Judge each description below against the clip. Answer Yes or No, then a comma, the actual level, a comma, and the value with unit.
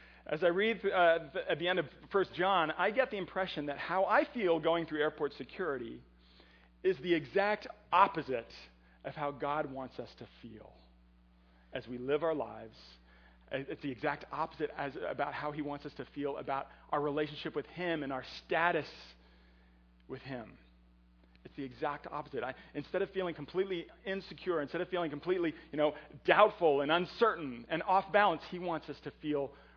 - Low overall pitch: No, medium, 150 Hz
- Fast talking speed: No, average, 175 wpm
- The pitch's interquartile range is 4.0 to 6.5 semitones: Yes, average, 5.2 semitones